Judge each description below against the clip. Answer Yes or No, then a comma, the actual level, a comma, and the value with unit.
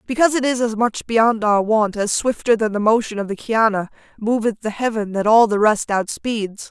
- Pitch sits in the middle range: No, high, 220 Hz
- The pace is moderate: No, fast, 215 wpm